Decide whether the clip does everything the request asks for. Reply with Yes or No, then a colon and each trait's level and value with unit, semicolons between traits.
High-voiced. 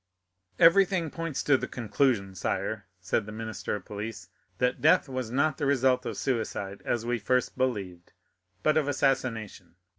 No: low, 120 Hz